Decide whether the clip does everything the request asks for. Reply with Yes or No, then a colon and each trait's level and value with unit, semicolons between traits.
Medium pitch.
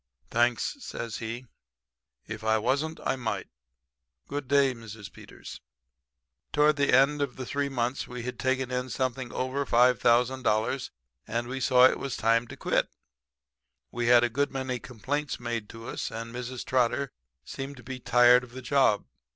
No: low, 125 Hz